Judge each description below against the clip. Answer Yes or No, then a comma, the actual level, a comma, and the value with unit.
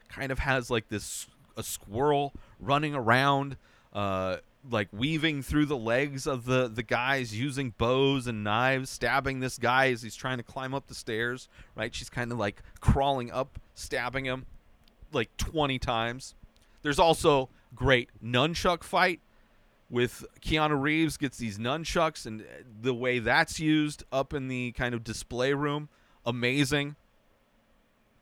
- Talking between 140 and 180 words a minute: Yes, average, 150 wpm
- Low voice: Yes, low, 130 Hz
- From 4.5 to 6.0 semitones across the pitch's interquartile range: No, average, 3.2 semitones